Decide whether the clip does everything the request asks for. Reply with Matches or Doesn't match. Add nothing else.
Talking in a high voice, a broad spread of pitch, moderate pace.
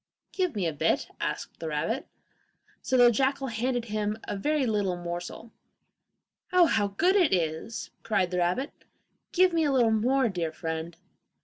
Matches